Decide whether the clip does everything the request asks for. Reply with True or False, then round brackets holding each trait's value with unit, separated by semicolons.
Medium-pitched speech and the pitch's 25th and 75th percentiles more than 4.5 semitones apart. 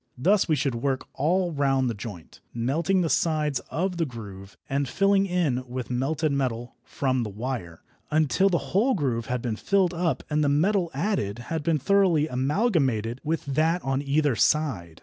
True (145 Hz; 5.3 semitones)